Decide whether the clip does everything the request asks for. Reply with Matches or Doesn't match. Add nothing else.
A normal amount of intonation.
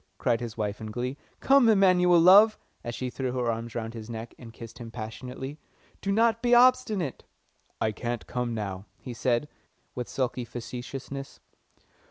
Doesn't match